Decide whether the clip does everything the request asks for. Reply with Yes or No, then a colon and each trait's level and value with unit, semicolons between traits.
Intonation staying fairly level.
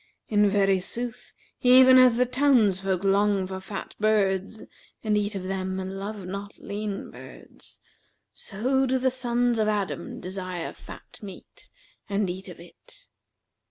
No: average, 3.6 semitones